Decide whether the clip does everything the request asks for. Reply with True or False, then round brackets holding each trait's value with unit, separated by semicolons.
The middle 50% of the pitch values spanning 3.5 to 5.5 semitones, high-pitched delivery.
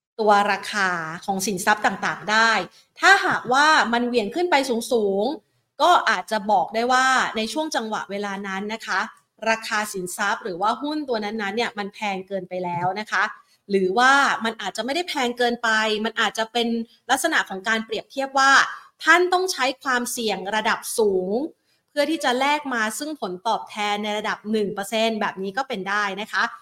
True (3.9 semitones; 220 Hz)